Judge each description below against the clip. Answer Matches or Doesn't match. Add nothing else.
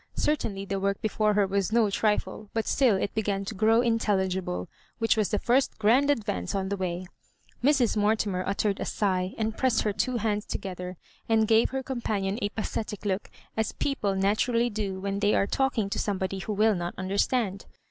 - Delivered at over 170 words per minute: Matches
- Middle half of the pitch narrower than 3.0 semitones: Matches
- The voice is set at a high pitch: Matches